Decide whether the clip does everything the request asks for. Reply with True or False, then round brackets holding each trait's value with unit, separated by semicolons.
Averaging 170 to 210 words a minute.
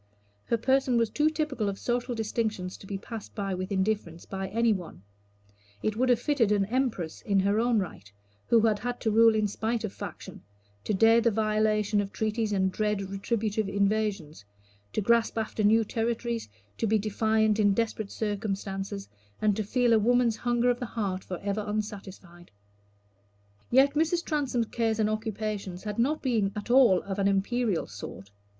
True (175 wpm)